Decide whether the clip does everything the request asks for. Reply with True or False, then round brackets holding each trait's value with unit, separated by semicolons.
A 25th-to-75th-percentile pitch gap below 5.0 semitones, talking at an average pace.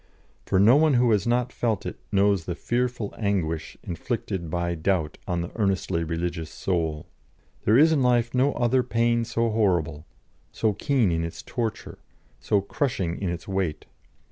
False (5.6 semitones; 165 wpm)